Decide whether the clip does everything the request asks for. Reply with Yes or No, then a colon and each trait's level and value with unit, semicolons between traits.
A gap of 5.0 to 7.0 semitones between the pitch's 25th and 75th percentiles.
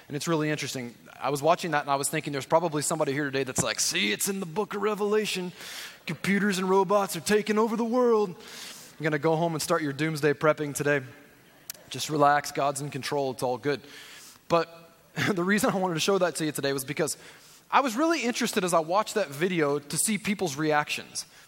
Yes: wide, 5.4 semitones